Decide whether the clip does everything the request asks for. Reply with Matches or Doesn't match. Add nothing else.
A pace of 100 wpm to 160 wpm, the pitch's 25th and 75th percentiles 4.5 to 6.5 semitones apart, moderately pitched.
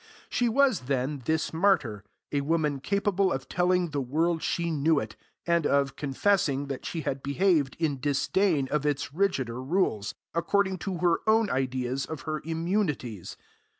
Matches